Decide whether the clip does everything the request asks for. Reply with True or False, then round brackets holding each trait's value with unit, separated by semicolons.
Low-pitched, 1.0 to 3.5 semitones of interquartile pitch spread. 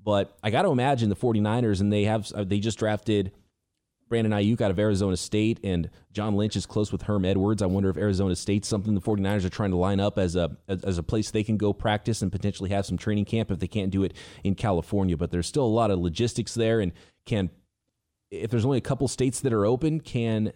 True (105 Hz; 2.5 semitones)